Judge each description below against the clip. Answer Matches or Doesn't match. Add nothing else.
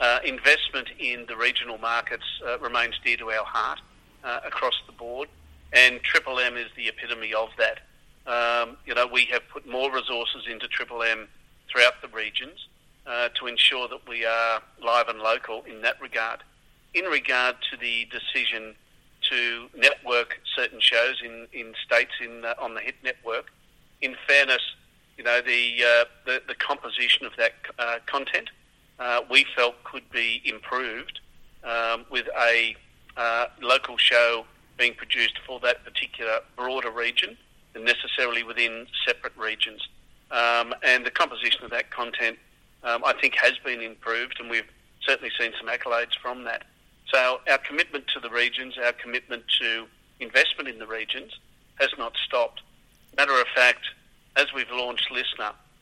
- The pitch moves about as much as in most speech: Doesn't match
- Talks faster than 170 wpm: Doesn't match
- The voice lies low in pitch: Matches